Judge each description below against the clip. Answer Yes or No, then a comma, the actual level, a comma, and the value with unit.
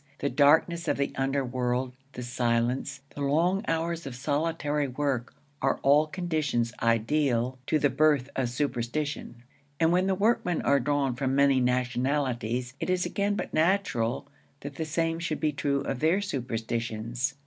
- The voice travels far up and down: No, average, 4.2 semitones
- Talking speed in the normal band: Yes, average, 155 wpm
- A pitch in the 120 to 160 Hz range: Yes, medium, 140 Hz